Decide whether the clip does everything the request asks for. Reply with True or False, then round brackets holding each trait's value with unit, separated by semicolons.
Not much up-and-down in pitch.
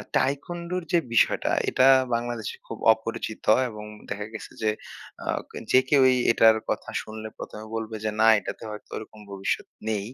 True (2.0 semitones)